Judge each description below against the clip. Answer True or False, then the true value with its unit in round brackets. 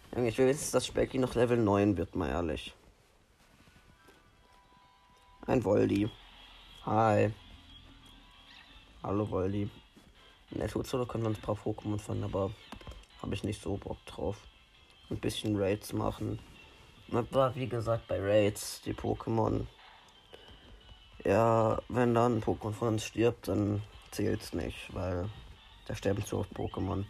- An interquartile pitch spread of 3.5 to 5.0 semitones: False (2.7 semitones)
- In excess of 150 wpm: False (135 wpm)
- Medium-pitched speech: False (105 Hz)